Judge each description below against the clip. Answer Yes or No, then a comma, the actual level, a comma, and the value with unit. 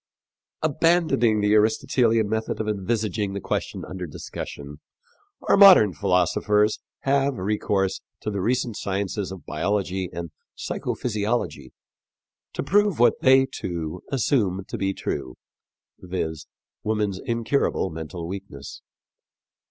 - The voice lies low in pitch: Yes, low, 105 Hz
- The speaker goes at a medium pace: No, slow, 120 wpm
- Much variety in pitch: No, average, 4.2 semitones